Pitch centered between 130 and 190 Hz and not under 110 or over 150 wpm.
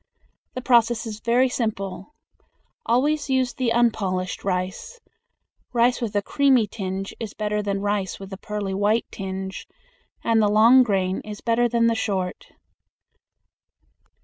No: high, 215 Hz; average, 140 wpm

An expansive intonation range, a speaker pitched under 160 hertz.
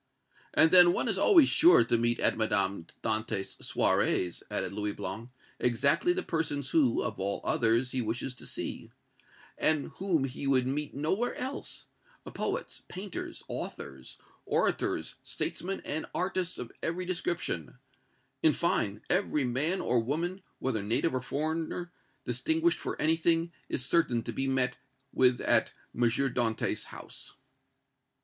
Yes: wide, 6.2 semitones; medium, 140 Hz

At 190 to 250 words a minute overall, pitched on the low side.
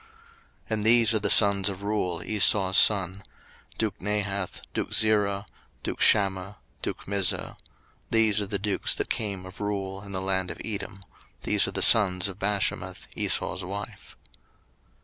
No: average, 155 wpm; low, 100 Hz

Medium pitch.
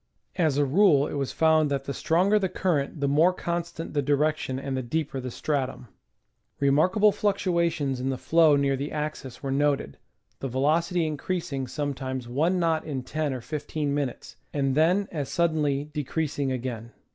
Yes: medium, 145 Hz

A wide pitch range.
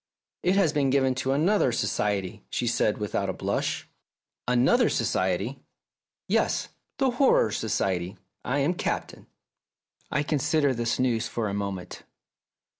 Yes: wide, 5.9 semitones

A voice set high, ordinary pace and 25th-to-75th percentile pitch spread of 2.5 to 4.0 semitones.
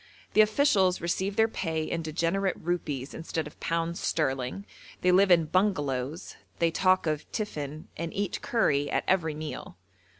No: medium, 170 Hz; average, 155 wpm; average, 3.7 semitones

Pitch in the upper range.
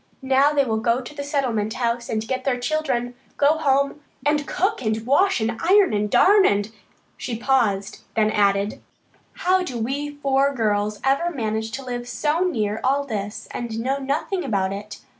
Yes: very high, 255 Hz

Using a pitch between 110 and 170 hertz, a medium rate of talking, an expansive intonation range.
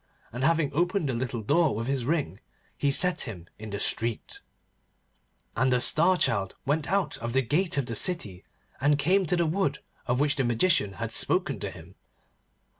Yes: medium, 140 Hz; average, 190 wpm; wide, 6.4 semitones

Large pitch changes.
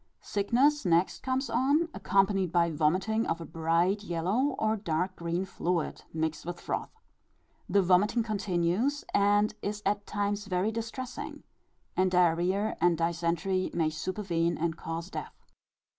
No: average, 3.8 semitones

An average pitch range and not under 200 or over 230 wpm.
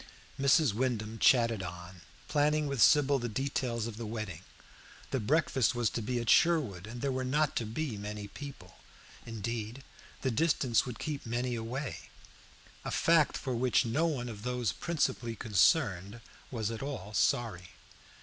No: average, 4.2 semitones; average, 160 wpm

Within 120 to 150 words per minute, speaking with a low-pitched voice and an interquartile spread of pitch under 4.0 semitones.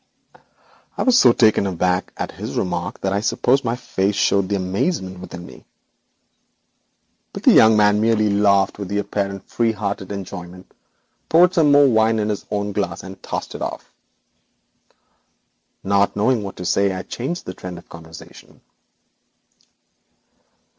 Yes: average, 145 wpm; low, 100 Hz; average, 2.8 semitones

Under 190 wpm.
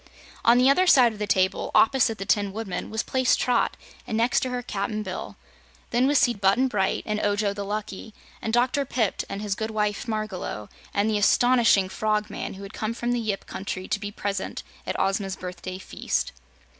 No: average, 195 wpm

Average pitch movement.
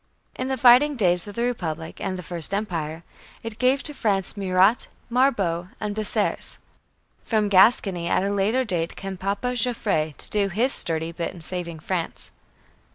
Yes: average, 5.0 semitones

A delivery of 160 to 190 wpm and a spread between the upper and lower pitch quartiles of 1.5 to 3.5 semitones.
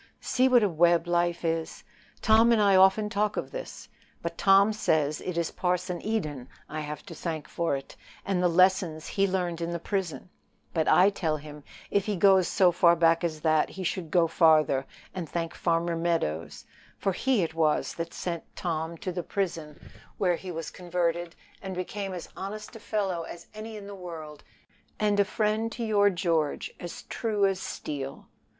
Yes: average, 185 wpm; average, 3.2 semitones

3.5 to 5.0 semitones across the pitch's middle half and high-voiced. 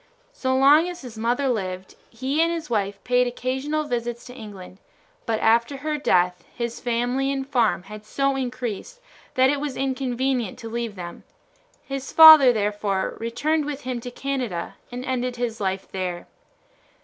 Yes: average, 3.8 semitones; high, 245 Hz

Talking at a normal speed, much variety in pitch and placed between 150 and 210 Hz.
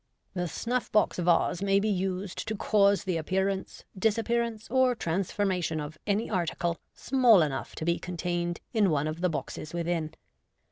No: average, 170 wpm; average, 3.7 semitones; medium, 185 Hz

